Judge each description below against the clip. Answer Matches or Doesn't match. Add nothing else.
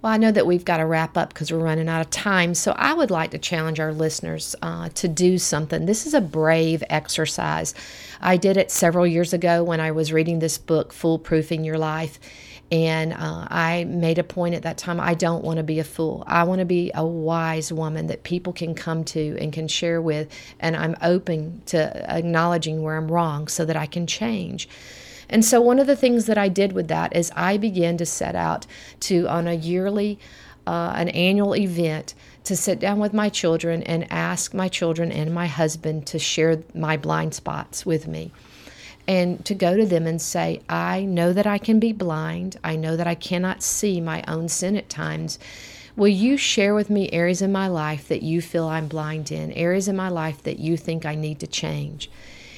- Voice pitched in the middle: Matches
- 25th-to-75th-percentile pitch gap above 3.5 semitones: Doesn't match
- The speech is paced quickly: Matches